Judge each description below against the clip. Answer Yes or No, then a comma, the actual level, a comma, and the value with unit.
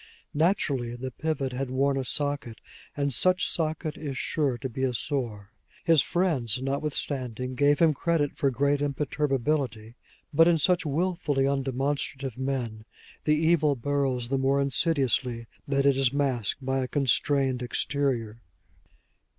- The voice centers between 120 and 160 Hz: Yes, medium, 140 Hz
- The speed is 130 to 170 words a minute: Yes, average, 140 wpm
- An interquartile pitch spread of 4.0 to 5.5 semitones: No, narrow, 2.4 semitones